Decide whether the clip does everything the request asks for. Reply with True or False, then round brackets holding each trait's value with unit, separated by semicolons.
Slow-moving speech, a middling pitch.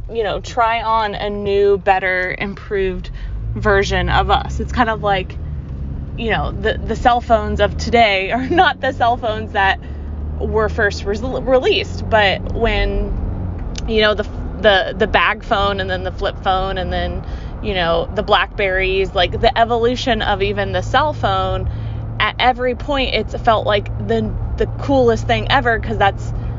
False (165 wpm; 175 Hz)